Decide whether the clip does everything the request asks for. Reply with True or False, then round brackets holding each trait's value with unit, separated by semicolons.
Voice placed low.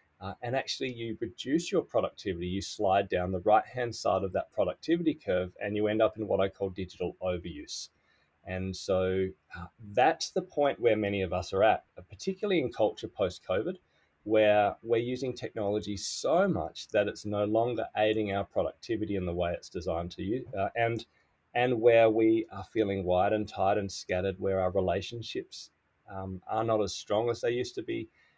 True (105 Hz)